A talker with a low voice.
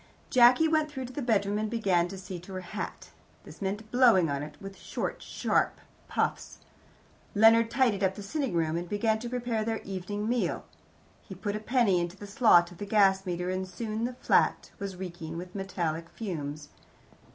No: high, 200 Hz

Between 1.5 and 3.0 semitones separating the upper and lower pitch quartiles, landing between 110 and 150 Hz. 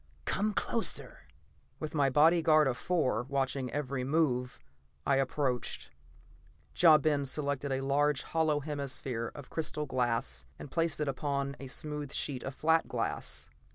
Yes: narrow, 2.5 semitones; medium, 140 Hz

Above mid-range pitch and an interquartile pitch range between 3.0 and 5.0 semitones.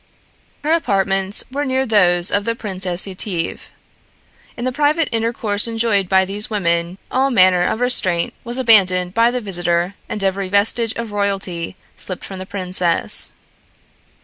Yes: high, 200 Hz; average, 3.9 semitones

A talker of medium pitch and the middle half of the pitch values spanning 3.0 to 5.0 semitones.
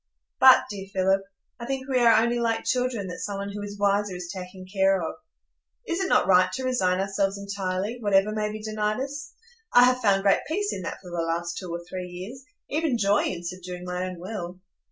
No: high, 200 Hz; average, 4.2 semitones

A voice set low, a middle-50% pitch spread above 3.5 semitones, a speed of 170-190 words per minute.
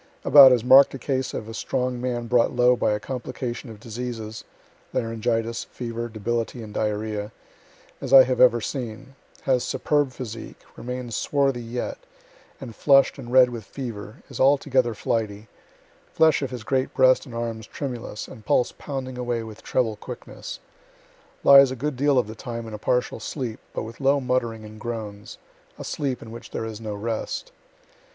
No: low, 120 Hz; narrow, 2.6 semitones; average, 175 wpm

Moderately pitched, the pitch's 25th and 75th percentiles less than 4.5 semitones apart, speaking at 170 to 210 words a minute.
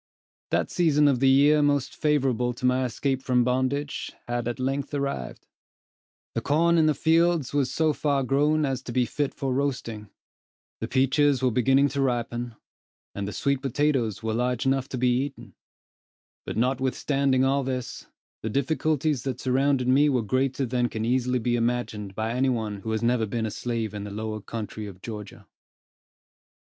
No: low, 130 Hz; average, 2.9 semitones; average, 175 wpm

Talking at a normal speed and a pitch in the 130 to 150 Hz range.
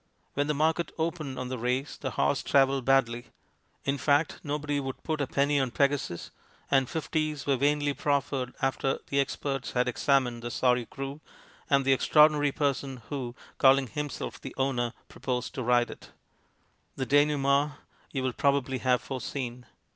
Yes: average, 160 wpm; low, 135 Hz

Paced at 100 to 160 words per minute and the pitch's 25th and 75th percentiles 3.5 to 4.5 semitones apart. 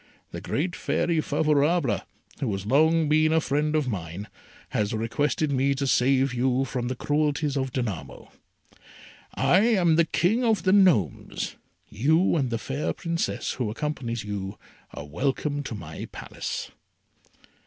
No: average, 145 wpm; average, 5.1 semitones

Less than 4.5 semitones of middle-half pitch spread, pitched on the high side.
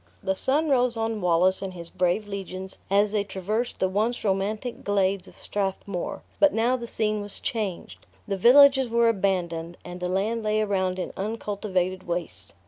Yes: average, 3.2 semitones; high, 200 Hz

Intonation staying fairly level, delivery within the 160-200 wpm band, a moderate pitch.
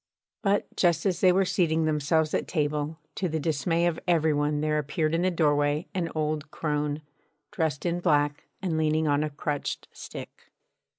Yes: narrow, 2.3 semitones; average, 175 wpm; medium, 155 Hz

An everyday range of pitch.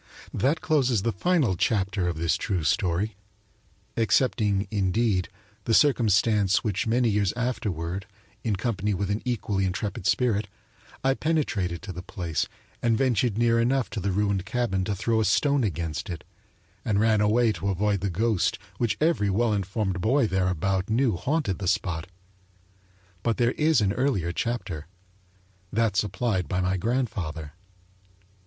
Yes: average, 4.0 semitones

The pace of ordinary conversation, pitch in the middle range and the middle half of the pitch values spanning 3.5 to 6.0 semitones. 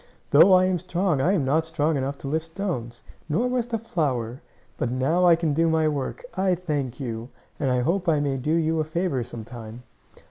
No: fast, 215 wpm; medium, 155 Hz; average, 5.1 semitones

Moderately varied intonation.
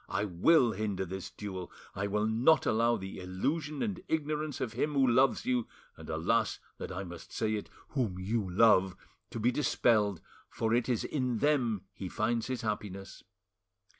Yes: average, 4.7 semitones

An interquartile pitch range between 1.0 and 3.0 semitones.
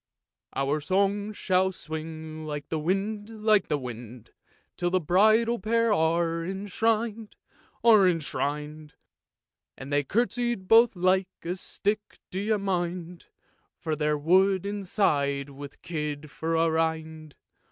No: average, 5.0 semitones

